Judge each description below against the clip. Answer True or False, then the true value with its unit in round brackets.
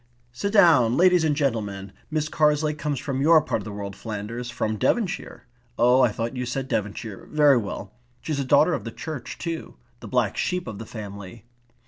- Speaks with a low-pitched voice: True (125 Hz)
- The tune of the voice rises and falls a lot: True (5.9 semitones)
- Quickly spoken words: False (190 wpm)